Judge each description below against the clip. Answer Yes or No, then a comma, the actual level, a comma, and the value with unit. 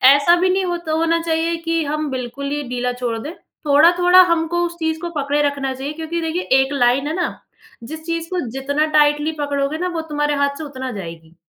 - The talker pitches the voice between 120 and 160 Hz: No, very high, 300 Hz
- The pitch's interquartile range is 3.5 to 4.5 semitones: No, average, 3.1 semitones